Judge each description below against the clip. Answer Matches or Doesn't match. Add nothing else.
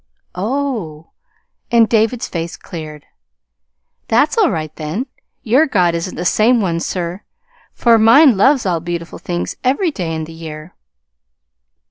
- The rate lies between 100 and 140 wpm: Matches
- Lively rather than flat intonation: Matches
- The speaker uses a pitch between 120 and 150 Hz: Doesn't match